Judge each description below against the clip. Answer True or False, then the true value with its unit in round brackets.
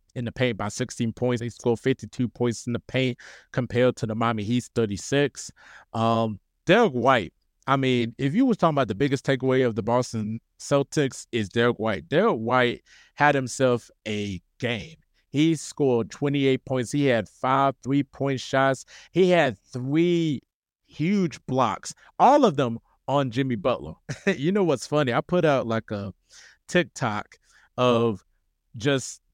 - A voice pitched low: True (125 Hz)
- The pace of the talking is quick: False (155 wpm)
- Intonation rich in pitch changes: False (3.4 semitones)